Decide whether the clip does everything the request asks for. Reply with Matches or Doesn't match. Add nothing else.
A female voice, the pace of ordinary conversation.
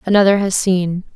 Matches